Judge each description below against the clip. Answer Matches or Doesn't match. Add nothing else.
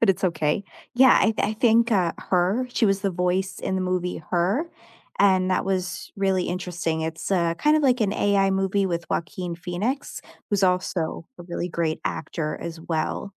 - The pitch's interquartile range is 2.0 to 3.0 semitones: Matches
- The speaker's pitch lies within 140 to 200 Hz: Matches